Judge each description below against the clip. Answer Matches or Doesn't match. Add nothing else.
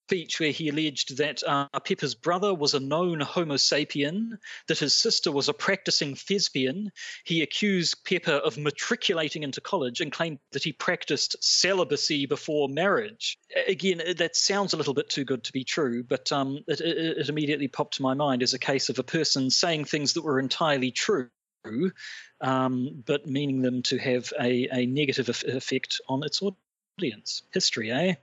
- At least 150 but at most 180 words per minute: Matches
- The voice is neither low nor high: Matches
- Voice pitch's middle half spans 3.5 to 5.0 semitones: Matches